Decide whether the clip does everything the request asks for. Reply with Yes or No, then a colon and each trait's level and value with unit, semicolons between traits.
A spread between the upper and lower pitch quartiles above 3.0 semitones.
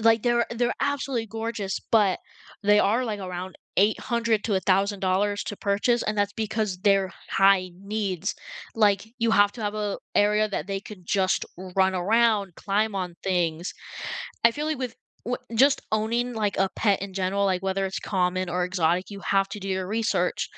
No: average, 2.7 semitones